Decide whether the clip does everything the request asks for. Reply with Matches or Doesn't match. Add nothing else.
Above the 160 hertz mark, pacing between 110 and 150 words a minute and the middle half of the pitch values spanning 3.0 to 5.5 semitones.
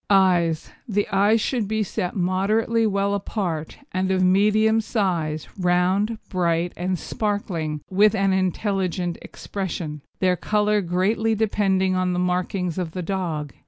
Doesn't match